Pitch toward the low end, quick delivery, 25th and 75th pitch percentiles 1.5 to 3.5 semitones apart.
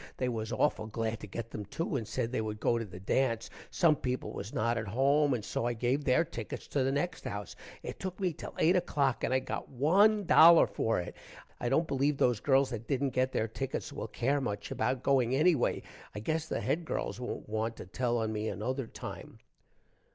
No: low, 125 Hz; fast, 220 wpm; average, 4.3 semitones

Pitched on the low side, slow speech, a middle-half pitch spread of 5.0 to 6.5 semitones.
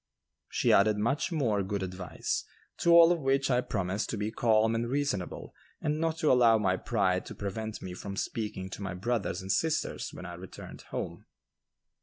No: low, 110 Hz; average, 185 wpm; wide, 5.4 semitones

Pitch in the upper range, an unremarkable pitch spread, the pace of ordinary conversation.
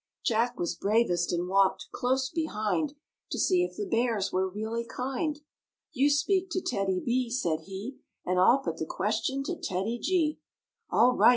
No: high, 240 Hz; wide, 6.4 semitones; average, 170 wpm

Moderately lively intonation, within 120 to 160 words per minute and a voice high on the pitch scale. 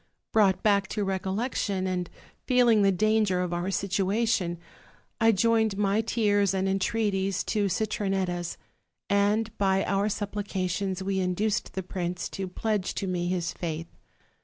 No: narrow, 2.3 semitones; average, 140 wpm; high, 195 Hz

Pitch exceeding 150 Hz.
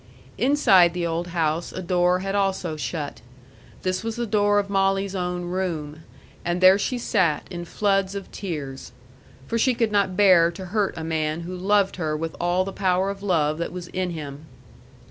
Yes: medium, 185 Hz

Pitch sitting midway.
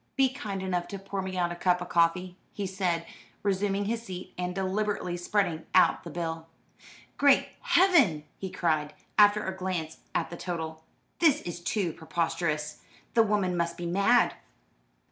Yes: medium, 180 Hz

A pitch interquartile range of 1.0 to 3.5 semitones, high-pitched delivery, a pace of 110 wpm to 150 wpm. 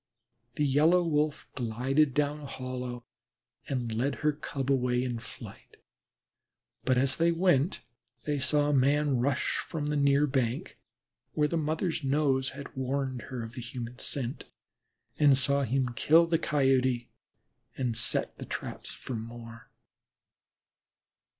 No: average, 2.9 semitones; low, 135 Hz; average, 145 wpm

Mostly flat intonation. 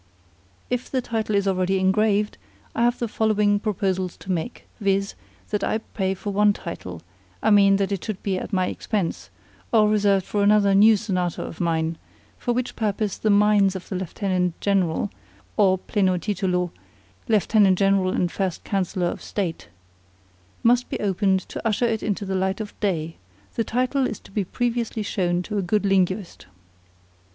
Yes: narrow, 2.3 semitones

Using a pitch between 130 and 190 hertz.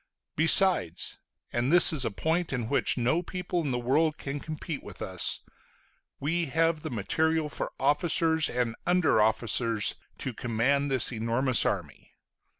Yes: medium, 140 Hz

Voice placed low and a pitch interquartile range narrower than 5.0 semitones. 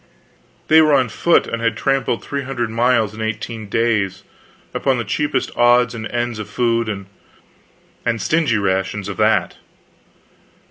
Yes: low, 115 Hz; average, 2.8 semitones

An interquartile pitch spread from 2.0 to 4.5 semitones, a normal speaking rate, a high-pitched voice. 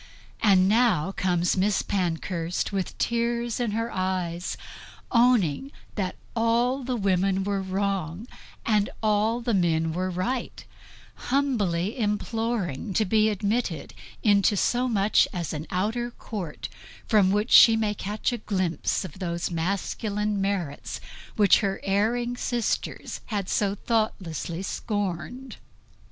No: average, 3.7 semitones; slow, 125 wpm; high, 200 Hz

